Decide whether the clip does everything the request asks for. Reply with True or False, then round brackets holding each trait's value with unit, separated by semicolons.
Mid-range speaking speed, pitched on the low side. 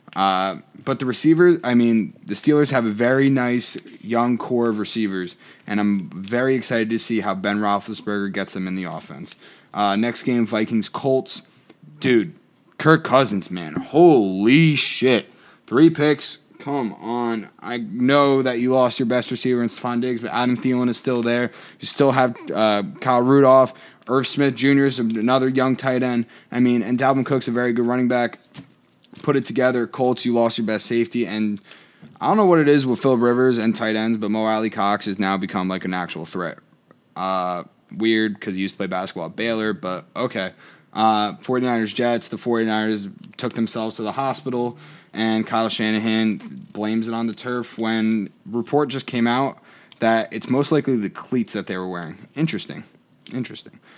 True (185 wpm; 120 Hz)